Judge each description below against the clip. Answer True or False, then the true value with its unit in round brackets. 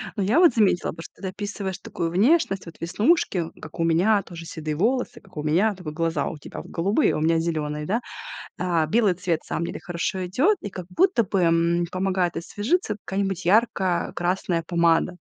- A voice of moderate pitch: True (180 Hz)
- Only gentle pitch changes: False (3.6 semitones)